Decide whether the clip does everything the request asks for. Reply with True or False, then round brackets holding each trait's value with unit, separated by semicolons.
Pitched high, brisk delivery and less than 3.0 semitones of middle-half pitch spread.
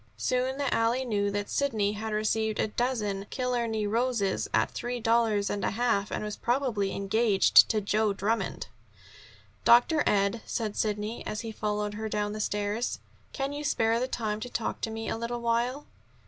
False (220 Hz; 175 wpm; 2.5 semitones)